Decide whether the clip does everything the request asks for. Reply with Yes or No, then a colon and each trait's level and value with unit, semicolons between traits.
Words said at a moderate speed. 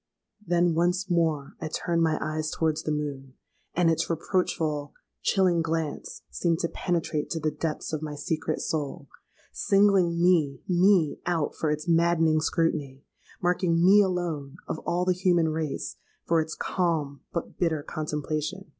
Yes: average, 145 wpm